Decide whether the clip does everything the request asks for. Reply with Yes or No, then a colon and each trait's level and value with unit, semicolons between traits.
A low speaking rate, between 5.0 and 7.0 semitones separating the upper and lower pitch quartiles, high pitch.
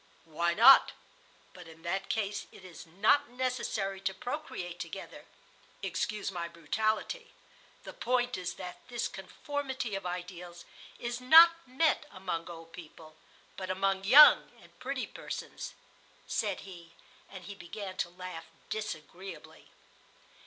Yes: slow, 130 wpm; wide, 5.6 semitones; high, 195 Hz